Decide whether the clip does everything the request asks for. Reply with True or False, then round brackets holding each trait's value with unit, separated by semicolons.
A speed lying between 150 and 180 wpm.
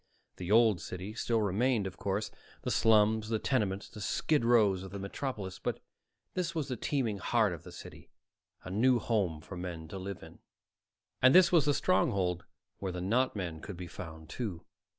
False (190 wpm)